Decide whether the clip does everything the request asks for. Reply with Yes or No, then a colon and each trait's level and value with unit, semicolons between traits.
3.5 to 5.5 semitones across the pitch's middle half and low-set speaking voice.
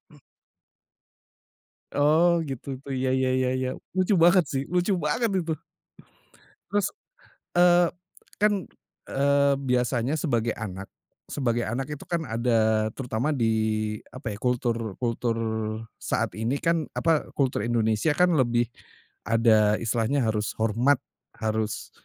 Yes: average, 5.0 semitones; low, 130 Hz